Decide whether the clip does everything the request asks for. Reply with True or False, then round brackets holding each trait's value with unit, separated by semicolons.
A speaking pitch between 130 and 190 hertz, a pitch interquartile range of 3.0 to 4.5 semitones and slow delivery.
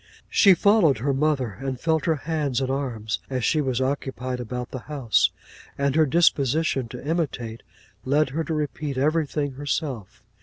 False (140 Hz; 3.3 semitones; 160 wpm)